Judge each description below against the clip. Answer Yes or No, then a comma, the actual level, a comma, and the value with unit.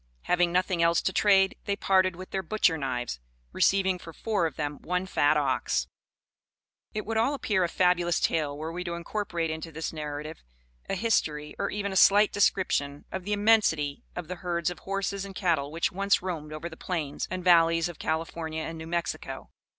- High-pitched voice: No, medium, 175 Hz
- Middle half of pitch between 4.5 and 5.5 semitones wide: No, average, 3.3 semitones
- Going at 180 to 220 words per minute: Yes, average, 190 wpm